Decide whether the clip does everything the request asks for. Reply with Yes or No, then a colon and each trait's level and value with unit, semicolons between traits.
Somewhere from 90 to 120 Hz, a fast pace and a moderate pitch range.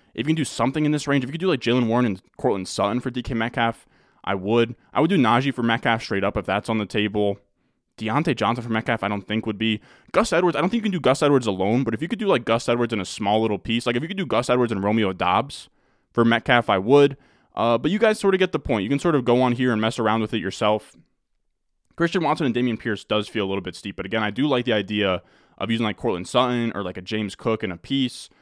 Yes: low, 115 Hz; fast, 285 wpm; average, 3.6 semitones